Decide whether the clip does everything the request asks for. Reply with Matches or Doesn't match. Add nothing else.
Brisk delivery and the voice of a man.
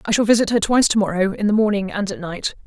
Doesn't match